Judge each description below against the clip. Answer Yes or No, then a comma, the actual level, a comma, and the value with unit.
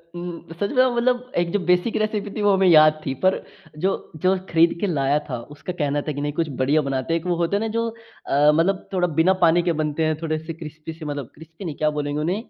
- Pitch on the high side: No, medium, 165 Hz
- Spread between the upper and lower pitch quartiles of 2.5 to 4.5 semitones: Yes, average, 3.8 semitones